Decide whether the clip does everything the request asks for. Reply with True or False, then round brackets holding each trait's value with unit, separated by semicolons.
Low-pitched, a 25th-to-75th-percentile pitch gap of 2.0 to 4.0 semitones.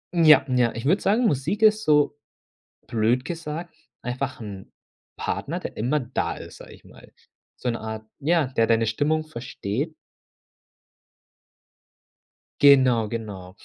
False (130 Hz; 5.2 semitones)